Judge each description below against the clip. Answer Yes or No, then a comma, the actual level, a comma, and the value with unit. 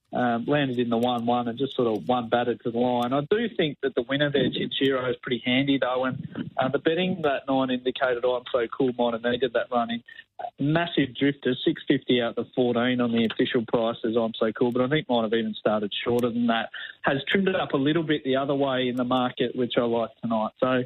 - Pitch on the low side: Yes, low, 125 Hz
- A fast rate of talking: Yes, fast, 245 wpm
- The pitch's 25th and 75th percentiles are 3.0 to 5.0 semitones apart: No, narrow, 2.6 semitones